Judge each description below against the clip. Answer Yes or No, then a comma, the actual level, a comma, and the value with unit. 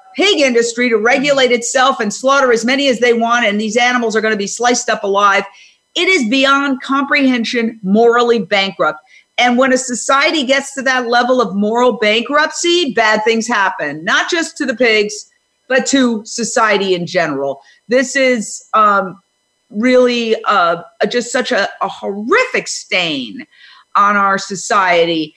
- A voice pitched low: No, high, 240 Hz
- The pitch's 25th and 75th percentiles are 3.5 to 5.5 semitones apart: Yes, average, 3.8 semitones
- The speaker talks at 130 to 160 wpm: Yes, average, 155 wpm